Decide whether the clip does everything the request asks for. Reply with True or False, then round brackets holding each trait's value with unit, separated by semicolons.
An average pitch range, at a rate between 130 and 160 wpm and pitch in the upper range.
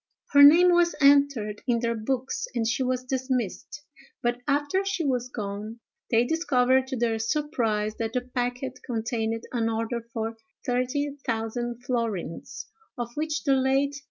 True (3.5 semitones; 155 wpm; 245 Hz)